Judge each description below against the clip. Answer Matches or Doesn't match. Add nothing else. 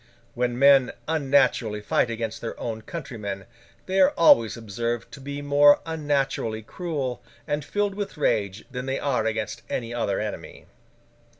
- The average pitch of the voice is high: Doesn't match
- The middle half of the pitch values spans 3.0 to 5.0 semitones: Matches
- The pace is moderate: Matches